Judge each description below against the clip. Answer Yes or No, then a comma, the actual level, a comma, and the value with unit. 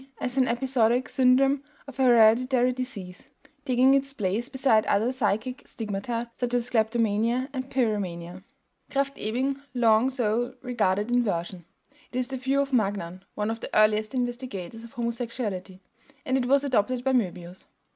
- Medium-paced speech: Yes, average, 150 wpm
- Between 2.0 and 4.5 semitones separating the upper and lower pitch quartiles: Yes, average, 3.4 semitones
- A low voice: No, high, 240 Hz